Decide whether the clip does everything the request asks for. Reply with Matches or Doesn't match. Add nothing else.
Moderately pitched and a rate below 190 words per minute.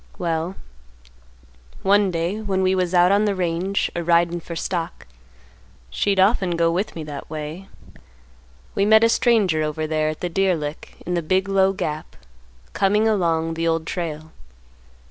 Matches